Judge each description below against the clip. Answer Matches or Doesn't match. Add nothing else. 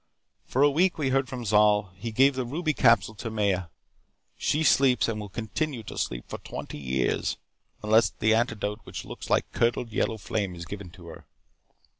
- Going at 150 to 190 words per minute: Matches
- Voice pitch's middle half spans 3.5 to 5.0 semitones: Matches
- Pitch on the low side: Matches